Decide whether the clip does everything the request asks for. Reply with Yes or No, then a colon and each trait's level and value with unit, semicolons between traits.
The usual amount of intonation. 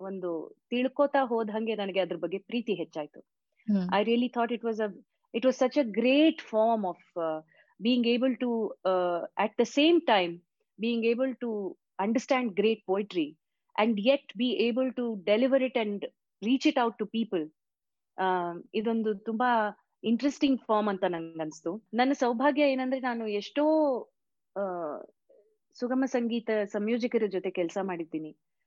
Yes: average, 4.9 semitones